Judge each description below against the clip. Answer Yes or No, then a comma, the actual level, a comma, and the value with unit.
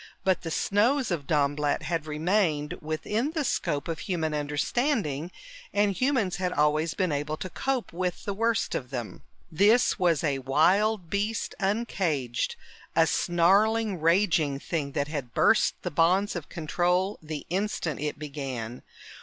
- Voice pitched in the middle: Yes, medium, 170 Hz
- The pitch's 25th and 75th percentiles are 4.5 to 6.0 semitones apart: Yes, average, 5.3 semitones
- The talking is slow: No, average, 145 wpm